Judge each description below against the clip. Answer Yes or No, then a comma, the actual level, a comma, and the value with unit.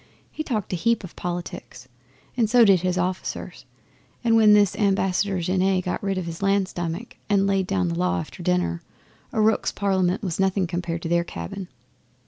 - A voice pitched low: No, medium, 185 Hz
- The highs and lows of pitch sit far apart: No, average, 2.7 semitones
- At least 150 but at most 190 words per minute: Yes, average, 185 wpm